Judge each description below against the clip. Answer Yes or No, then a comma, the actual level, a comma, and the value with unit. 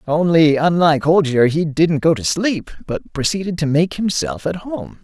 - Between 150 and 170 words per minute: No, average, 180 wpm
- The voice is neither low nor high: Yes, medium, 160 Hz